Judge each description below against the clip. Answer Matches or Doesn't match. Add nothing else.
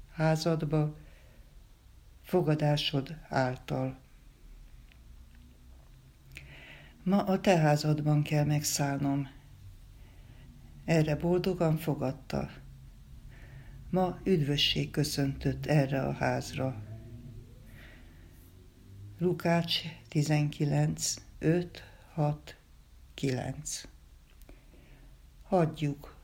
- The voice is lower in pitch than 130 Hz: Doesn't match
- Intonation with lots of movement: Matches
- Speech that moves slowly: Matches